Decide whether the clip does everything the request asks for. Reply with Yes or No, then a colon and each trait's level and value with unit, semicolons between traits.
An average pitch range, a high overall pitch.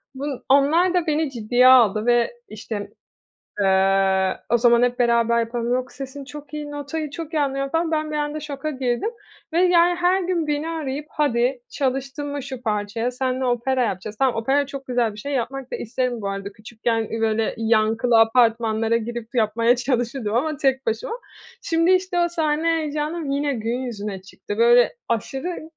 Yes: average, 4.5 semitones; very high, 255 Hz